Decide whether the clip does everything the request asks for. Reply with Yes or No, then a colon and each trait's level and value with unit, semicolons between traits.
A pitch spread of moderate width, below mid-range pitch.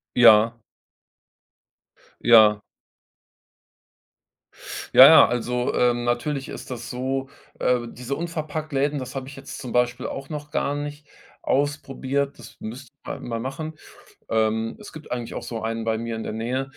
Yes: average, 3.3 semitones; low, 125 Hz